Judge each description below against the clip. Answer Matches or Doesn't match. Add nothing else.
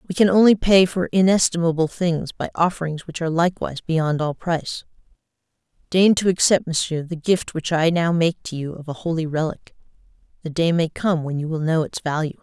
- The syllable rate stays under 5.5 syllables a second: Doesn't match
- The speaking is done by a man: Doesn't match